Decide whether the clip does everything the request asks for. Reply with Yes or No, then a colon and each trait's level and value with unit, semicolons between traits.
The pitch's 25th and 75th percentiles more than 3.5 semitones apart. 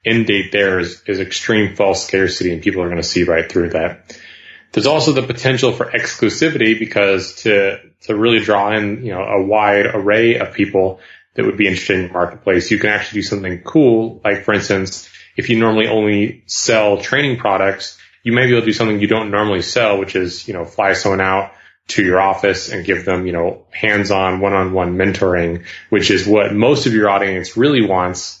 No: narrow, 2.5 semitones